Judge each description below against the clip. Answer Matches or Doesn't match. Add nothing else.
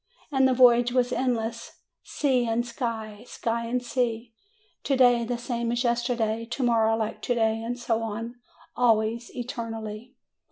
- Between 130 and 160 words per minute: Matches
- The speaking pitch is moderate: Doesn't match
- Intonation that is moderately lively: Doesn't match